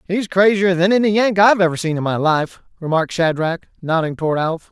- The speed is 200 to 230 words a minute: Yes, fast, 205 wpm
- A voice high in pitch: No, medium, 175 Hz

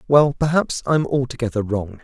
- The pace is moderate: Yes, average, 150 wpm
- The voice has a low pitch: Yes, low, 130 Hz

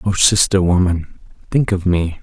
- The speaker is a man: Yes, male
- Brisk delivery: No, average, 160 wpm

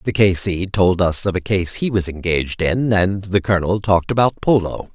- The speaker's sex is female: No, male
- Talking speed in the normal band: No, fast, 220 wpm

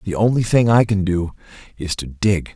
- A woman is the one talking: No, male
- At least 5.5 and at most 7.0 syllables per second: No, 5.0 syllables/s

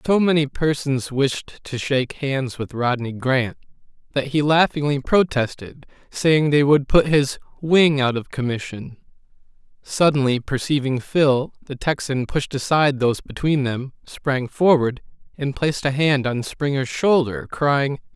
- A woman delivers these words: No, male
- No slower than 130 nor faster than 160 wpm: Yes, average, 140 wpm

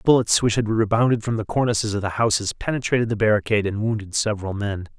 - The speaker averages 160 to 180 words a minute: No, fast, 205 wpm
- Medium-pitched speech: No, low, 110 Hz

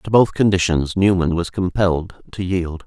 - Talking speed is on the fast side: No, average, 170 wpm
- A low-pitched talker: Yes, very low, 90 Hz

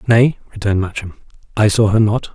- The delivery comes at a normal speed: Yes, average, 180 wpm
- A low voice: Yes, low, 105 Hz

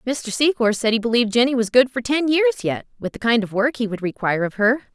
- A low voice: No, high, 240 Hz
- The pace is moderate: No, fast, 265 wpm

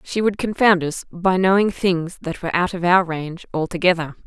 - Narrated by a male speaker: No, female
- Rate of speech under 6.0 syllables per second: Yes, 5.4 syllables/s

